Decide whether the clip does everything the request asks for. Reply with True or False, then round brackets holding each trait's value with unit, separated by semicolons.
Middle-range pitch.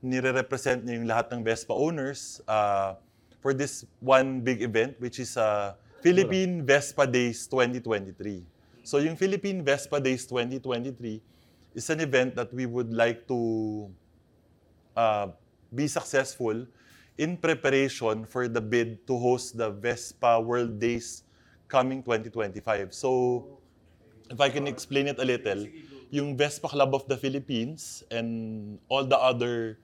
False (125 Hz)